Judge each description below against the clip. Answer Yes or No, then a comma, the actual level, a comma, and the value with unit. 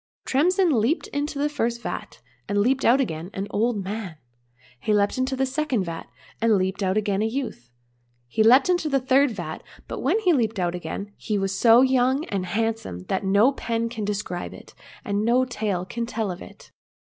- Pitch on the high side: Yes, high, 225 Hz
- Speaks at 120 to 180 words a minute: No, average, 200 wpm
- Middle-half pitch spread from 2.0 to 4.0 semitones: No, average, 5.0 semitones